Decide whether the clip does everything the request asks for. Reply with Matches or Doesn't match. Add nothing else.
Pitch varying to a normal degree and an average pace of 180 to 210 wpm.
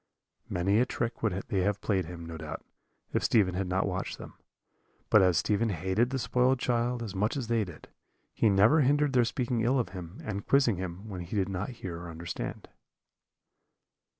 Matches